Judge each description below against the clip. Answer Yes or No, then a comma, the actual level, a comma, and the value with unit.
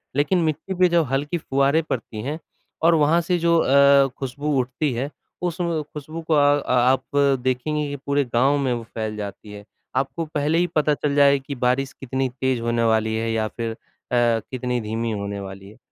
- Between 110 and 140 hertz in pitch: Yes, low, 135 Hz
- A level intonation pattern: No, average, 4.4 semitones